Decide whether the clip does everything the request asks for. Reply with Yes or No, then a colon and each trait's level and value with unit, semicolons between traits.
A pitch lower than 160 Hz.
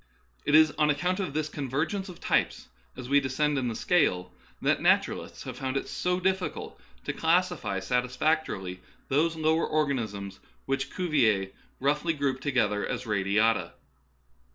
Yes: medium, 140 Hz